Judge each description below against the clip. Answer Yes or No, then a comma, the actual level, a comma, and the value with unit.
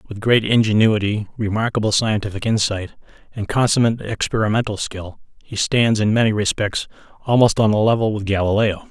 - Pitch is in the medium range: No, low, 110 Hz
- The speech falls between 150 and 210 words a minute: No, average, 140 wpm